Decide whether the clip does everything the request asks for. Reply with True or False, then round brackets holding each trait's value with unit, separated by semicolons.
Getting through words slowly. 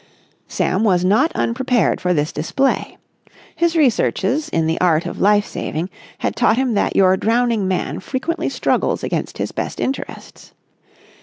False (150 wpm)